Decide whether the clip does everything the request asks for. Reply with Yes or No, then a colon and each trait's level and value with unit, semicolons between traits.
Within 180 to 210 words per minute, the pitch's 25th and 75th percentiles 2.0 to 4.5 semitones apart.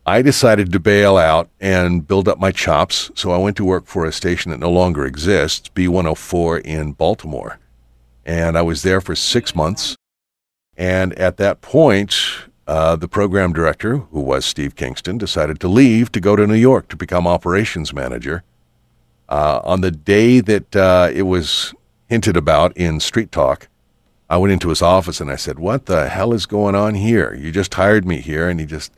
Yes: average, 190 wpm; average, 3.8 semitones